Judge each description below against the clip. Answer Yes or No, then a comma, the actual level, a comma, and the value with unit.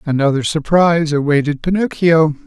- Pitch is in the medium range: Yes, medium, 155 Hz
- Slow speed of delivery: Yes, slow, 95 wpm